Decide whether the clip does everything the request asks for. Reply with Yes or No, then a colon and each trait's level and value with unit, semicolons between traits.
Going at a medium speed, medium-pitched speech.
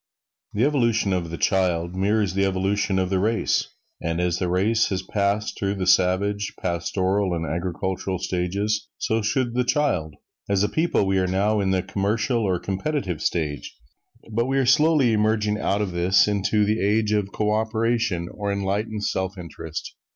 No: average, 175 wpm; low, 100 Hz